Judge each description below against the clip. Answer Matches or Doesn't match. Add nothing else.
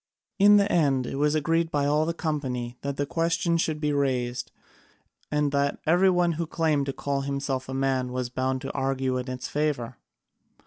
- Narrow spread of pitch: Doesn't match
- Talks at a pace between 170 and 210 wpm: Matches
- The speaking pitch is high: Doesn't match